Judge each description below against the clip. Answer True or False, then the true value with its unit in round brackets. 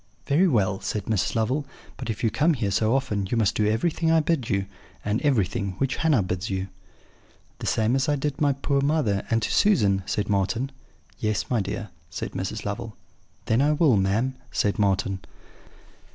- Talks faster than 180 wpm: True (190 wpm)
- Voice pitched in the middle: False (110 Hz)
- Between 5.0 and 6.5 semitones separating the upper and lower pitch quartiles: True (5.6 semitones)